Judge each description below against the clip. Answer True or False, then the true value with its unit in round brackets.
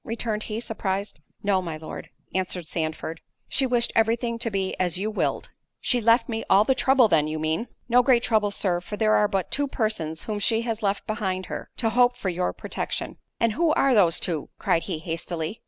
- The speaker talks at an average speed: False (210 wpm)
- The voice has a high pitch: True (210 Hz)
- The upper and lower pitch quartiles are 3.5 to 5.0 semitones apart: True (4.4 semitones)